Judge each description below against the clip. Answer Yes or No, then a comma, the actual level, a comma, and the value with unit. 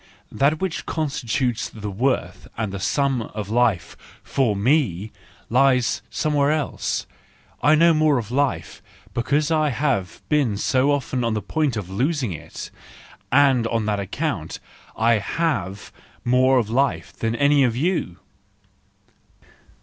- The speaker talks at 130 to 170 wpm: Yes, average, 140 wpm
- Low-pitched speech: Yes, low, 125 Hz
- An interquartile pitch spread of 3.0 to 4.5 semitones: No, average, 4.9 semitones